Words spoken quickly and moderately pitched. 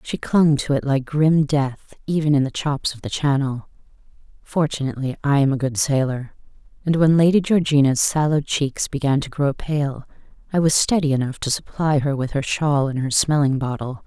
No: average, 190 wpm; medium, 145 Hz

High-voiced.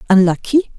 Yes: high, 220 Hz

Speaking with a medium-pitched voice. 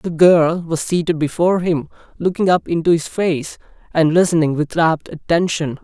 Yes: medium, 165 Hz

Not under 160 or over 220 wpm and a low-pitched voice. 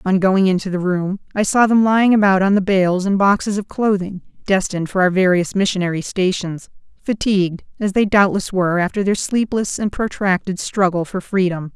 No: average, 185 wpm; high, 190 Hz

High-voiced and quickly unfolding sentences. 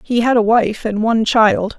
Yes: high, 225 Hz; fast, 235 wpm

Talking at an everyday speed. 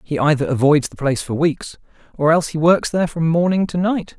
No: fast, 230 wpm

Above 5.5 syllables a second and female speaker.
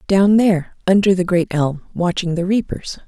No: 5.0 syllables/s; female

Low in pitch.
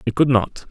Yes: low, 125 Hz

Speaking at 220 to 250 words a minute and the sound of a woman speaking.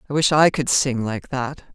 Yes: fast, 240 wpm; female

